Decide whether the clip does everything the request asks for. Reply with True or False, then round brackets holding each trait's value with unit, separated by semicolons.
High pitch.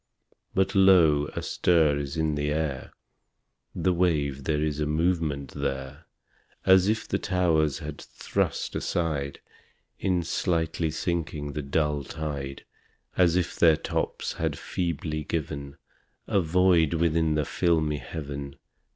False (80 Hz)